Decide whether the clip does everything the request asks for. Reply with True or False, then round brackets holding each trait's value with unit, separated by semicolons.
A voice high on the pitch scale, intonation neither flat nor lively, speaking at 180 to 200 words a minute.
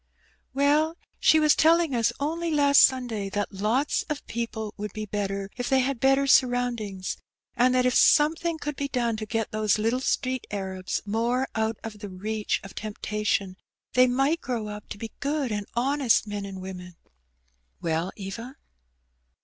False (230 Hz; 4.7 semitones; 165 wpm)